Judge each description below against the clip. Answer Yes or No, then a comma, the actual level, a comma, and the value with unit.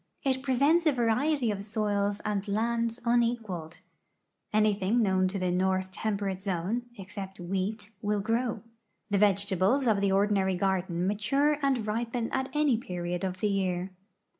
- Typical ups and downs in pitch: Yes, average, 3.6 semitones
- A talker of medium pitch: No, high, 205 Hz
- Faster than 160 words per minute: No, average, 145 wpm